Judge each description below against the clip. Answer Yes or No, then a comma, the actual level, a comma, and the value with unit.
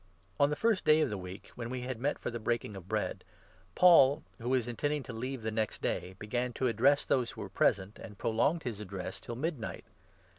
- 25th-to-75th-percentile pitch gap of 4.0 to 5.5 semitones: Yes, average, 4.3 semitones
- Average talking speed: No, fast, 225 wpm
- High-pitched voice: No, low, 120 Hz